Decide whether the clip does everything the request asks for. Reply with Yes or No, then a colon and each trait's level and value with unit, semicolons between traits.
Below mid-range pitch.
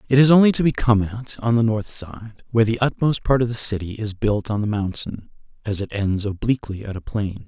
Yes: low, 110 Hz